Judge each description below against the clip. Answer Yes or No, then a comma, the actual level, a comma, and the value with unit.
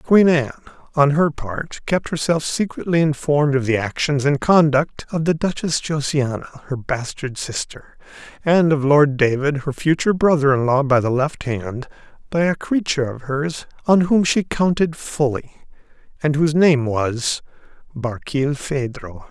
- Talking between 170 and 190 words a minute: No, average, 150 wpm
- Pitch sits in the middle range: Yes, medium, 145 Hz